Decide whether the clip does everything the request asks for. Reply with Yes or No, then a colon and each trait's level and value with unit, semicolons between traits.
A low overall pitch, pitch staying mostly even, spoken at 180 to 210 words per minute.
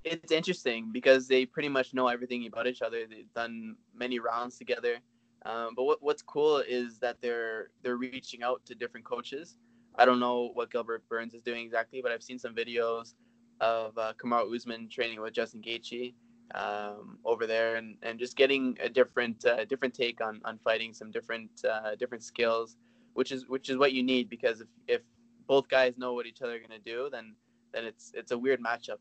Yes: low, 120 Hz; narrow, 2.2 semitones; fast, 205 wpm